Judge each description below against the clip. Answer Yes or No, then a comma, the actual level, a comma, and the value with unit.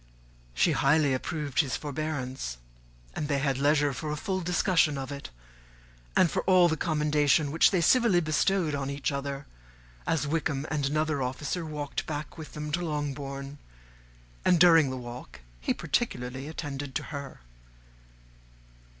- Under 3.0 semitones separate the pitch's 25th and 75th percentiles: Yes, narrow, 2.4 semitones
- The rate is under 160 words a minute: Yes, average, 150 wpm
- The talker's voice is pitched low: No, medium, 145 Hz